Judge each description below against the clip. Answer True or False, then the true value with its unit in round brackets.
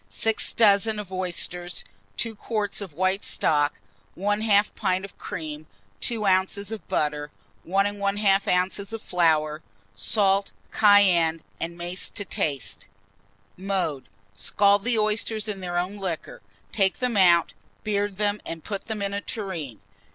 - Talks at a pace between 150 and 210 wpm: False (140 wpm)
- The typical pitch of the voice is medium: False (195 Hz)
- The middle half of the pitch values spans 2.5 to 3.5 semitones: True (3.1 semitones)